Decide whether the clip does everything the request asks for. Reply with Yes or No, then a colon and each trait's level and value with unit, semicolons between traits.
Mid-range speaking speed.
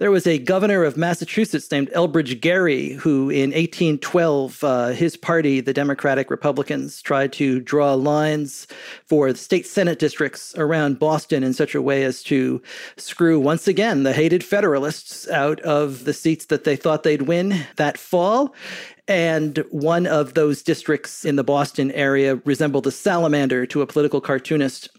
Yes: average, 165 wpm